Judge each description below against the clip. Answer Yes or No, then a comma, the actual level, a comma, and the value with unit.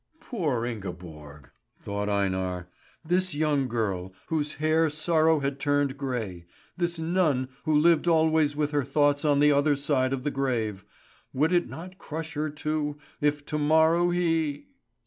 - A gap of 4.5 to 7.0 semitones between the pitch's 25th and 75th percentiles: No, average, 4.0 semitones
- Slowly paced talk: No, average, 150 wpm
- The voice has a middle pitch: Yes, medium, 145 Hz